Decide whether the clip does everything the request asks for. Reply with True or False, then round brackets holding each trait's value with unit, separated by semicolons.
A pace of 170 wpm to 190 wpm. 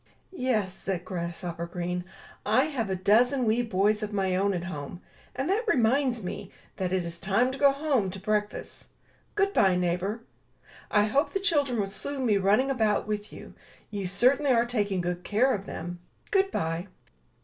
True (180 wpm)